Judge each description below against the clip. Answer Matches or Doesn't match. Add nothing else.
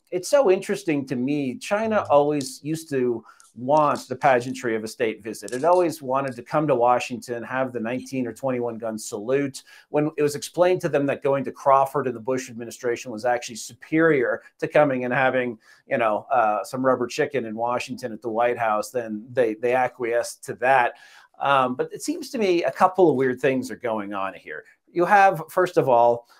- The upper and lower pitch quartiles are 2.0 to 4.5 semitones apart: Matches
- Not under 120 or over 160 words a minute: Doesn't match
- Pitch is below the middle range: Matches